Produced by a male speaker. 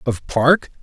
Yes: male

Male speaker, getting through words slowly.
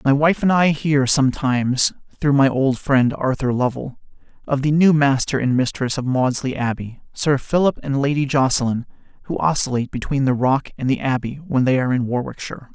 No: male; average, 185 wpm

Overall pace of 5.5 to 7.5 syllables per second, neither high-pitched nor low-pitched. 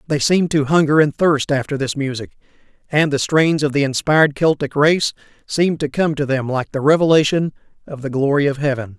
Yes: 5.6 syllables/s; medium, 145 Hz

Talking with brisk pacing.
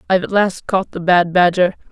Yes: fast, 250 wpm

